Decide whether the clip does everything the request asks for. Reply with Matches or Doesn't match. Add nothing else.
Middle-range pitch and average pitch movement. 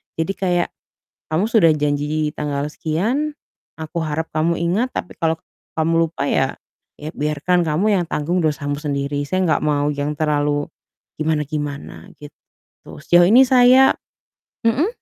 Matches